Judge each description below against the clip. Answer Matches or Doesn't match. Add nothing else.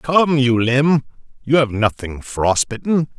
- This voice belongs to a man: Matches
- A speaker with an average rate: Matches